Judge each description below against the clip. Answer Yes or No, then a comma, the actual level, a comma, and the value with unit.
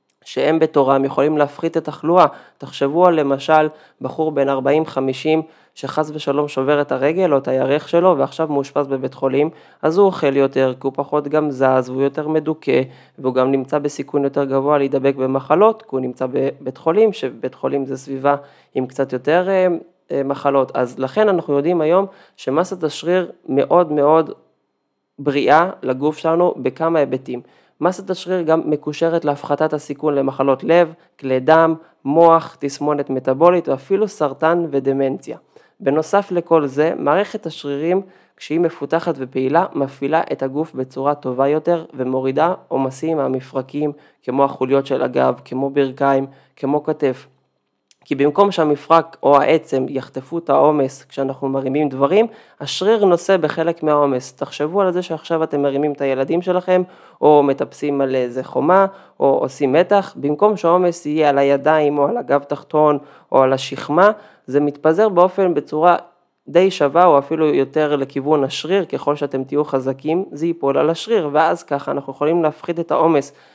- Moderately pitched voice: Yes, medium, 145 Hz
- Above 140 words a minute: Yes, fast, 150 wpm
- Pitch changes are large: No, average, 3.3 semitones